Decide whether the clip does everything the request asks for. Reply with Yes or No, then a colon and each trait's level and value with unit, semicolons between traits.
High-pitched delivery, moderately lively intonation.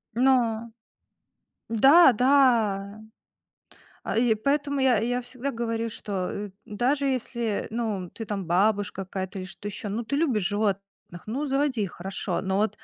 Yes: high, 225 Hz; average, 4.1 semitones